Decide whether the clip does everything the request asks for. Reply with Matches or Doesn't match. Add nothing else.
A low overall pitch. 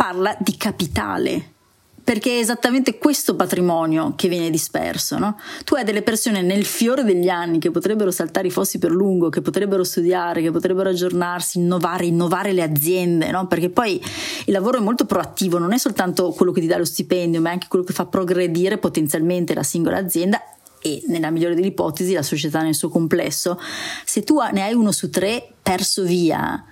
Doesn't match